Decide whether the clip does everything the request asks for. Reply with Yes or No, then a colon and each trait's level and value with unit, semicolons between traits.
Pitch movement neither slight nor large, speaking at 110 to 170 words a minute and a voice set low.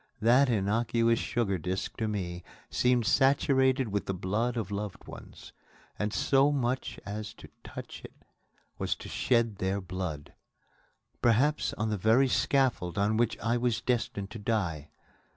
Yes: average, 3.8 semitones; average, 150 wpm; low, 110 Hz